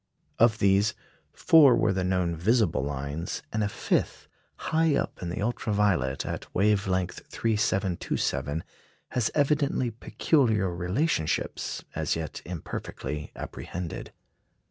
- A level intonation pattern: No, average, 4.9 semitones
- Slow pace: Yes, slow, 120 wpm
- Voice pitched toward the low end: Yes, low, 100 Hz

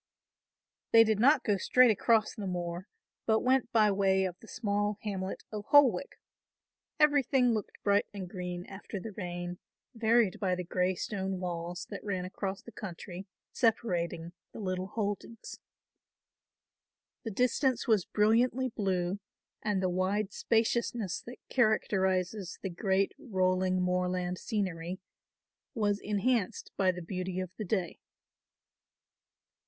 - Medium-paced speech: No, slow, 130 wpm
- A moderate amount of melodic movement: Yes, average, 3.4 semitones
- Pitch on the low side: No, high, 195 Hz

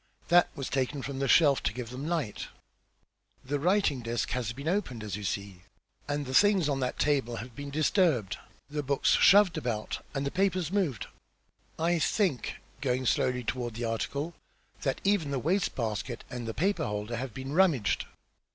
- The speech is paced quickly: No, average, 180 wpm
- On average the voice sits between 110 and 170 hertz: Yes, low, 135 Hz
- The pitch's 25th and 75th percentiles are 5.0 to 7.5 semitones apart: Yes, wide, 5.4 semitones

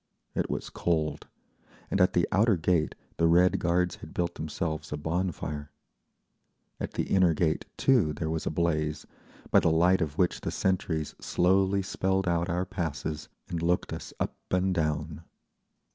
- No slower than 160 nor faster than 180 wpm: Yes, average, 165 wpm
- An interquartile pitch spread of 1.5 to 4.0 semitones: Yes, average, 2.8 semitones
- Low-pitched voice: Yes, very low, 85 Hz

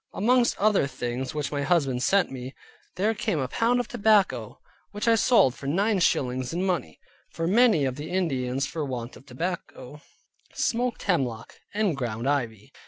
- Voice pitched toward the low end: No, medium, 150 Hz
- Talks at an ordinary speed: Yes, average, 170 wpm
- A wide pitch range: Yes, wide, 8.1 semitones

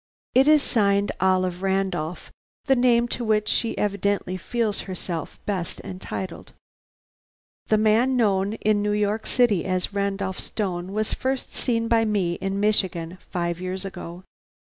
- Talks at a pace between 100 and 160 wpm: Yes, average, 140 wpm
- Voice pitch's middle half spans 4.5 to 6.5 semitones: No, average, 2.9 semitones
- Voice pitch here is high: Yes, high, 200 Hz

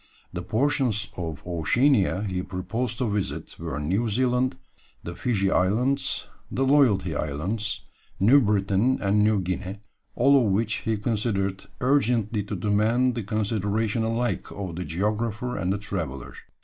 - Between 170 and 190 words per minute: No, average, 140 wpm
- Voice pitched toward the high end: No, low, 105 Hz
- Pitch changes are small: No, average, 3.9 semitones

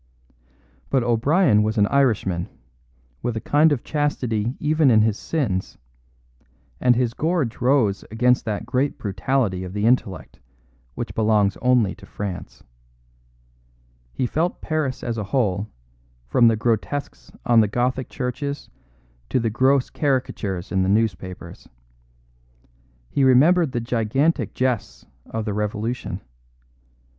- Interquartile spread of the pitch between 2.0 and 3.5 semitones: No, average, 4.3 semitones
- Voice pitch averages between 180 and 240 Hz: No, low, 120 Hz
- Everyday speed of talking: No, slow, 130 wpm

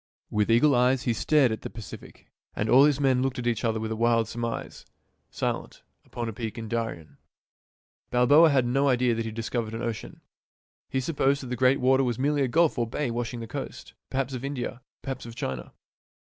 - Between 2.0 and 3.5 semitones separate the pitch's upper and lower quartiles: Yes, average, 2.7 semitones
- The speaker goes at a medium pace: No, fast, 220 wpm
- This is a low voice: Yes, low, 120 Hz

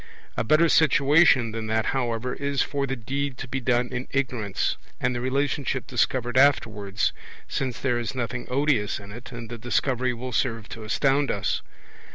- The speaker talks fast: No, average, 175 wpm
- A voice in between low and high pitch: No, low, 125 Hz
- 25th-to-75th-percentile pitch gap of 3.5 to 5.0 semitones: No, average, 3.0 semitones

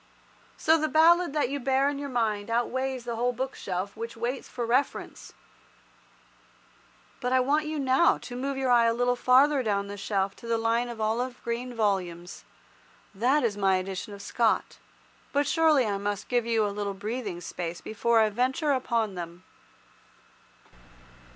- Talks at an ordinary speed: Yes, average, 170 wpm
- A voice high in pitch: Yes, high, 235 Hz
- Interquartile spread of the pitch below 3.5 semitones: No, average, 4.3 semitones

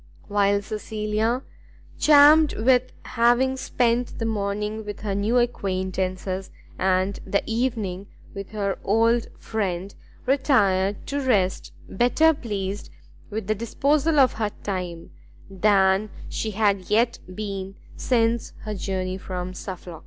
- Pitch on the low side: No, high, 210 Hz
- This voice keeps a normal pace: No, slow, 120 wpm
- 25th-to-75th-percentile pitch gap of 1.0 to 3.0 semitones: No, average, 3.6 semitones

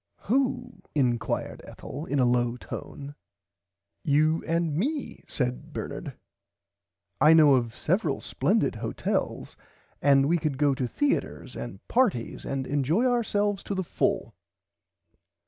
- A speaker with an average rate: No, slow, 125 wpm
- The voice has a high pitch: No, medium, 150 Hz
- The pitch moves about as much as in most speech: No, wide, 6.9 semitones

